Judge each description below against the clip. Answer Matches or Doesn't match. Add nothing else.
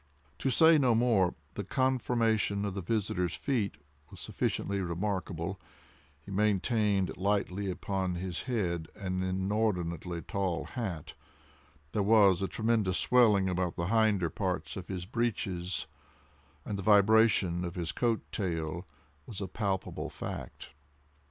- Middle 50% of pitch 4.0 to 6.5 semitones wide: Doesn't match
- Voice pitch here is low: Matches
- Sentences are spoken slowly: Matches